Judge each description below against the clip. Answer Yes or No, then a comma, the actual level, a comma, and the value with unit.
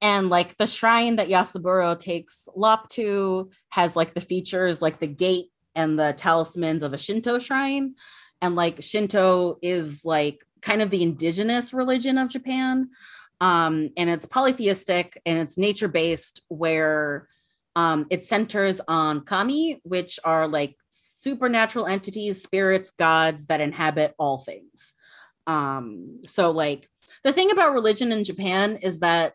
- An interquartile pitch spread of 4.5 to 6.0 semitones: Yes, average, 4.9 semitones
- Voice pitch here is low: No, medium, 185 Hz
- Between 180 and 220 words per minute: No, average, 145 wpm